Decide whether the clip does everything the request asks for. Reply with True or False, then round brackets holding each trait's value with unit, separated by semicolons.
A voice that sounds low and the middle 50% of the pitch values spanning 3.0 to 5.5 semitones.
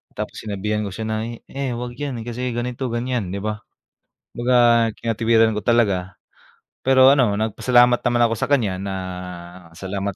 False (115 Hz; 2.6 semitones)